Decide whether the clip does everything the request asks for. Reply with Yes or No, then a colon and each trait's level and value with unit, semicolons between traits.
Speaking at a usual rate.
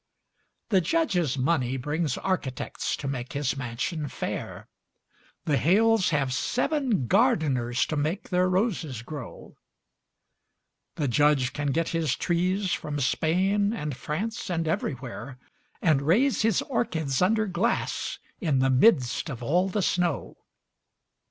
No: slow, 125 wpm